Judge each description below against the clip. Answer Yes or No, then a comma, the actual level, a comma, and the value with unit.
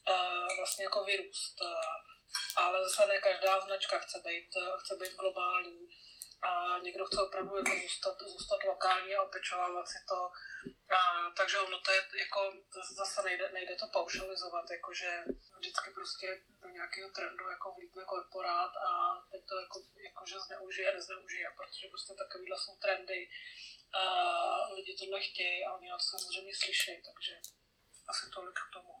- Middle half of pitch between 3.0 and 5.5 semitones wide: No, narrow, 2.4 semitones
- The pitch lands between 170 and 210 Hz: Yes, high, 190 Hz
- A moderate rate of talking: Yes, average, 155 wpm